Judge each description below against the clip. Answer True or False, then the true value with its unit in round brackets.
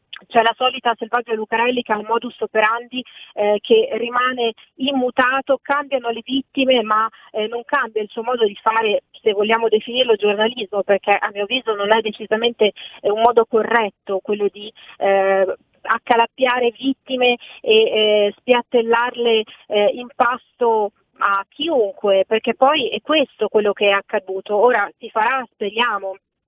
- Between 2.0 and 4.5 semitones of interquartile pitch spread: True (2.8 semitones)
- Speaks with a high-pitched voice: True (225 Hz)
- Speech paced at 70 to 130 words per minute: False (145 wpm)